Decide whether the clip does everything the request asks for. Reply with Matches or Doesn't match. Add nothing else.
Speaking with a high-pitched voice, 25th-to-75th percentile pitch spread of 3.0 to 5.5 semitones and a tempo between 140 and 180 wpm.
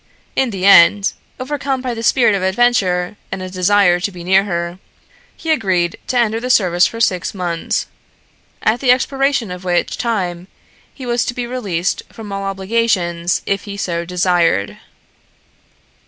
Matches